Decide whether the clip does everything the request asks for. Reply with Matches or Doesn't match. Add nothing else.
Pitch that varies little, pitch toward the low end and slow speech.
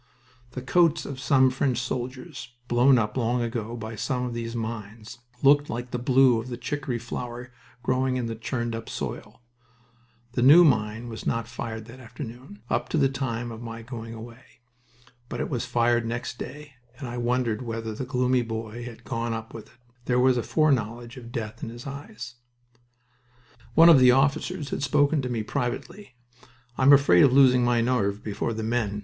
Doesn't match